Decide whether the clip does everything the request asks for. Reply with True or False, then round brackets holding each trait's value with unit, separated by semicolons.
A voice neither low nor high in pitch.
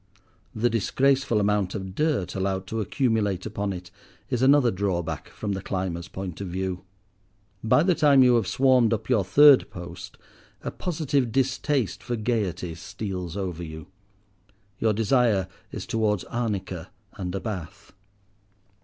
False (105 Hz)